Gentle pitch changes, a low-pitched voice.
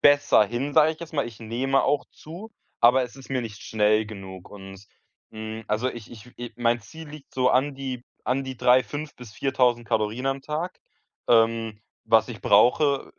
No: average, 3.7 semitones; low, 125 Hz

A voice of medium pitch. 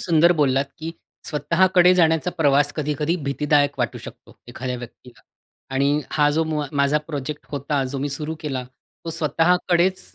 Yes: medium, 150 Hz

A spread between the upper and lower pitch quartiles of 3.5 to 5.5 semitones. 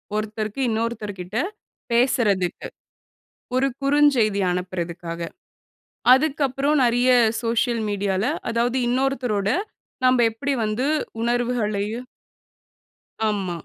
Yes: average, 3.9 semitones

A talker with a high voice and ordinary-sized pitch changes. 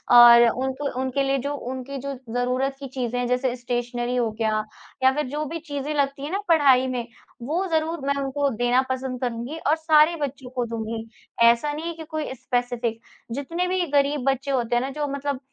Yes: very high, 265 Hz; average, 3.0 semitones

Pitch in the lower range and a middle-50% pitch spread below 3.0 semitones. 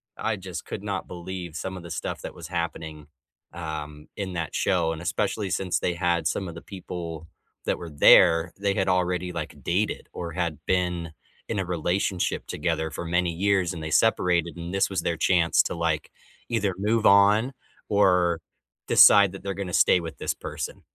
Yes: very low, 90 Hz; narrow, 2.5 semitones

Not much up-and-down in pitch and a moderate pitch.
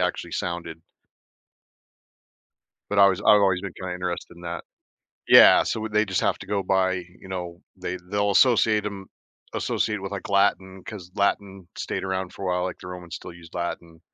No: narrow, 2.0 semitones; very low, 95 Hz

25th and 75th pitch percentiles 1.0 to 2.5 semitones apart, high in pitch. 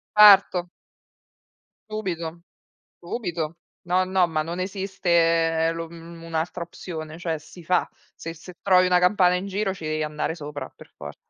No: narrow, 2.2 semitones; medium, 170 Hz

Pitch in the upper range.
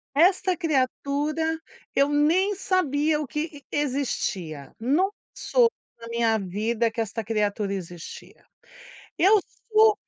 Yes: very high, 285 Hz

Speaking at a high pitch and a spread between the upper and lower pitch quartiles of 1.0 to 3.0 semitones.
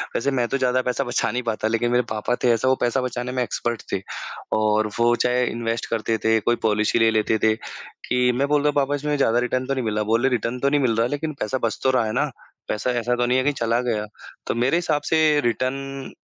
No: low, 125 Hz; narrow, 2.5 semitones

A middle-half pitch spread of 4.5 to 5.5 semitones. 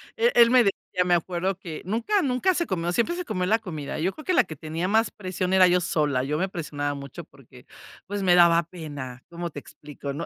Yes: average, 5.0 semitones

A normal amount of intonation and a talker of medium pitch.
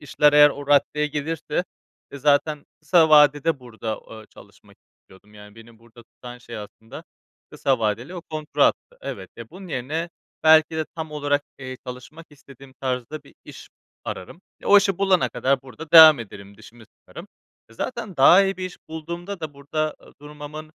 Yes: average, 4.4 semitones; medium, 145 Hz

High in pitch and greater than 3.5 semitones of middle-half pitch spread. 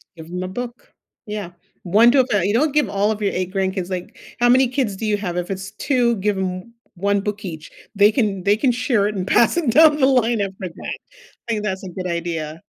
Yes: high, 205 Hz; average, 4.1 semitones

